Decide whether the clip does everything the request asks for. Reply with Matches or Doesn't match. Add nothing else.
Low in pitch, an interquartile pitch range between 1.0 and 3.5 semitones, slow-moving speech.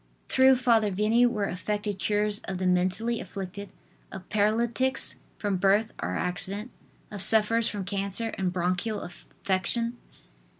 Doesn't match